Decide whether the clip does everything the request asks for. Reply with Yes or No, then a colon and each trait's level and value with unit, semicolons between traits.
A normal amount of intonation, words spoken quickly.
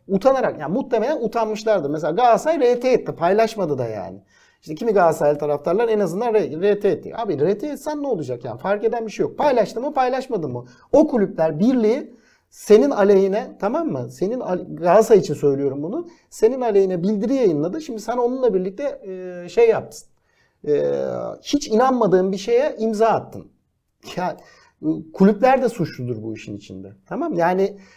No: wide, 6.5 semitones; fast, 155 wpm